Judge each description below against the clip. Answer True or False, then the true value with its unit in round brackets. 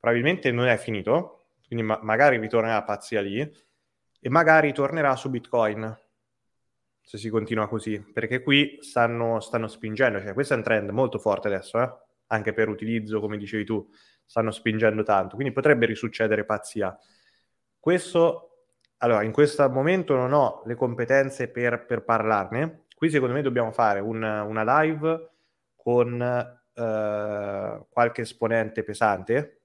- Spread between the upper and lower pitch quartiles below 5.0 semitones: True (3.9 semitones)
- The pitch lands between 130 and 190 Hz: False (120 Hz)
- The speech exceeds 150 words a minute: False (145 wpm)